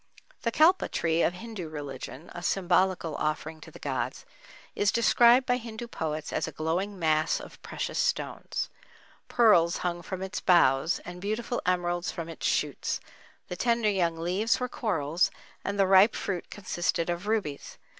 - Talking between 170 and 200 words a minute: No, average, 160 wpm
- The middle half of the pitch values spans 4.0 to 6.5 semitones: Yes, average, 4.4 semitones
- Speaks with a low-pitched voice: No, medium, 180 Hz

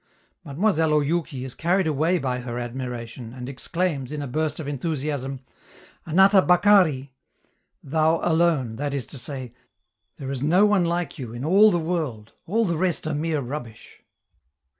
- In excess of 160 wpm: No, average, 155 wpm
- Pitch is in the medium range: Yes, medium, 150 Hz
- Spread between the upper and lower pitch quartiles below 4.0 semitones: No, average, 4.7 semitones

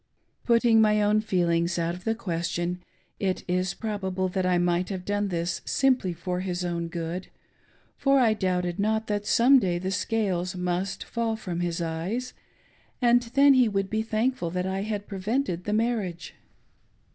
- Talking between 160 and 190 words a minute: Yes, average, 170 wpm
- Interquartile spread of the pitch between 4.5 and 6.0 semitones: No, average, 3.7 semitones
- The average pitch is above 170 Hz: Yes, high, 190 Hz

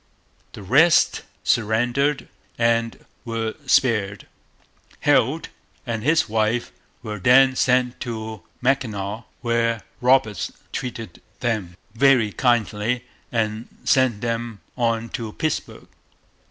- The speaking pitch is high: No, low, 115 Hz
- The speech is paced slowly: Yes, slow, 100 wpm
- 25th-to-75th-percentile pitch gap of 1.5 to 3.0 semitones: Yes, narrow, 2.4 semitones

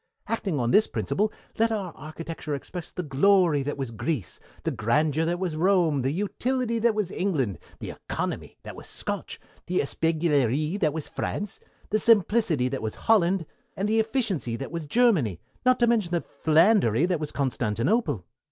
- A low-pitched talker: No, medium, 165 Hz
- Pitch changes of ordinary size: No, wide, 6.5 semitones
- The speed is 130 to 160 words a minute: No, average, 170 wpm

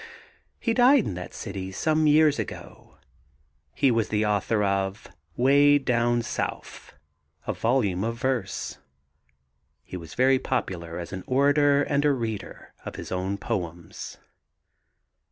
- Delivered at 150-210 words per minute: No, slow, 135 wpm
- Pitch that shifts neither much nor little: No, wide, 6.6 semitones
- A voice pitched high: No, low, 115 Hz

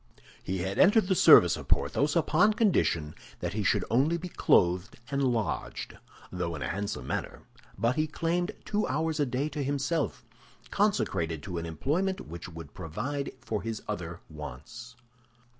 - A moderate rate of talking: Yes, average, 160 wpm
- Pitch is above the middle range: No, low, 120 Hz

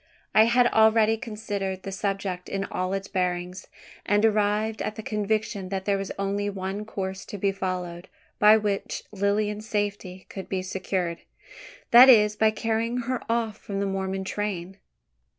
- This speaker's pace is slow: No, average, 160 wpm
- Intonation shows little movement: Yes, narrow, 2.1 semitones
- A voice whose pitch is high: Yes, high, 200 Hz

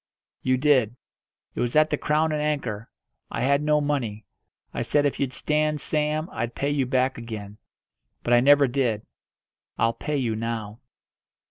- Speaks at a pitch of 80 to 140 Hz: Yes, low, 135 Hz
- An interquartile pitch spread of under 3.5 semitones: No, average, 4.4 semitones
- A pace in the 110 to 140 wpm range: No, average, 165 wpm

